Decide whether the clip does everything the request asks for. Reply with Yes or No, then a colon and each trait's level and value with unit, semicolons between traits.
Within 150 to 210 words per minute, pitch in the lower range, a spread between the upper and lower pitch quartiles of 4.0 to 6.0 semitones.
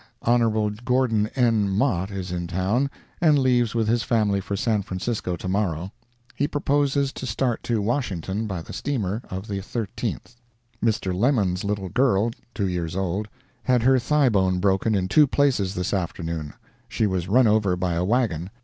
Yes: average, 170 wpm; low, 105 Hz; average, 4.6 semitones